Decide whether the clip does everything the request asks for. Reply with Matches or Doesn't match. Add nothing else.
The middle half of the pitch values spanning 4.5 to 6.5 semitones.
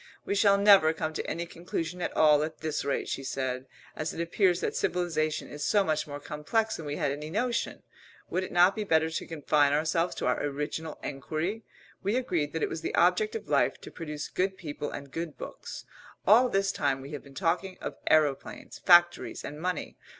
Doesn't match